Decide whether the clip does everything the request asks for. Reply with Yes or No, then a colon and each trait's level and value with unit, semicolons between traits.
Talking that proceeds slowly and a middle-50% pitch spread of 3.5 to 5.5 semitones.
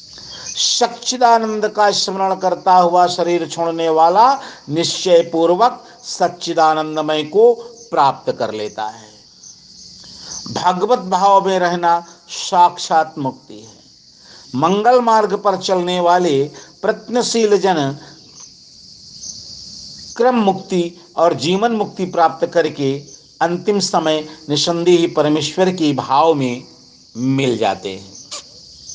Yes: slow, 95 wpm; average, 4.3 semitones